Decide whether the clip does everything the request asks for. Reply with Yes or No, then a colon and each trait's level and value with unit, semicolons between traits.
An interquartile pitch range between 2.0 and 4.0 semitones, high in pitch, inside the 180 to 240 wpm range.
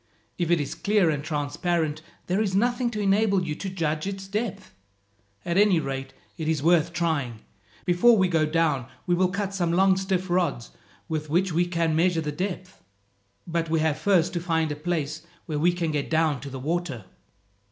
No: average, 3.3 semitones; medium, 170 Hz; average, 195 wpm